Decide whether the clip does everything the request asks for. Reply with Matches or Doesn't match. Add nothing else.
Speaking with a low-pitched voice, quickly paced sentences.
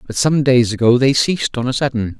Matches